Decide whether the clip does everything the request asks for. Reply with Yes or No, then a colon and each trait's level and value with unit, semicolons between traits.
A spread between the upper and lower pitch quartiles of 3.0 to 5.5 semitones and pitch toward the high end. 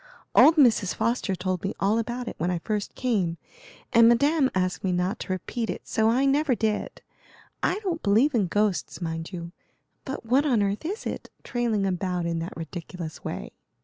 Yes: average, 5.2 semitones; high, 210 Hz